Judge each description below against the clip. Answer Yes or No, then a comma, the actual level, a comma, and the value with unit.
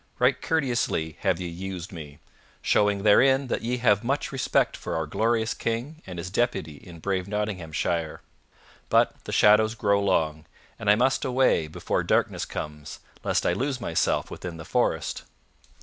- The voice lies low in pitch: Yes, low, 100 Hz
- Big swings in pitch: Yes, wide, 6.1 semitones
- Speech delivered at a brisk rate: No, average, 160 wpm